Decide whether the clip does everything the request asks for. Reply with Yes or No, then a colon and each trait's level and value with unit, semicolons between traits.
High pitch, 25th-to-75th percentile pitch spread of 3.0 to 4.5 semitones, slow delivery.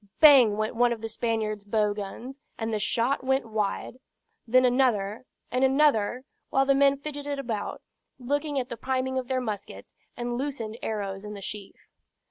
No: high, 240 Hz; average, 3.8 semitones; average, 170 wpm